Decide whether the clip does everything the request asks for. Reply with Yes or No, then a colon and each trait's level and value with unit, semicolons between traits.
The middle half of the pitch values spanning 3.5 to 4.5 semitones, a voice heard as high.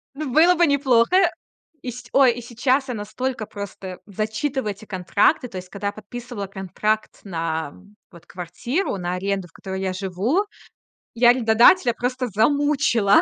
No: average, 4.9 semitones; high, 220 Hz